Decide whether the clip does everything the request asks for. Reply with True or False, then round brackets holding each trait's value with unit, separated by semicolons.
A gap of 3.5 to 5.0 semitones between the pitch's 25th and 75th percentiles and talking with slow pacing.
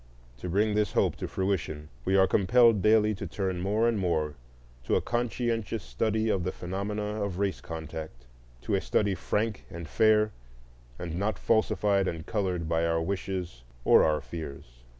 False (4.5 semitones; 165 wpm)